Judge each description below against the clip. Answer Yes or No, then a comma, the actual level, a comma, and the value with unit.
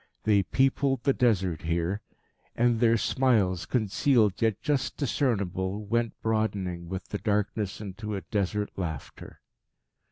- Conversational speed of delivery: No, slow, 125 wpm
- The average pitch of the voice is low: Yes, low, 105 Hz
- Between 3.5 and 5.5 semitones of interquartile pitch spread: Yes, average, 3.8 semitones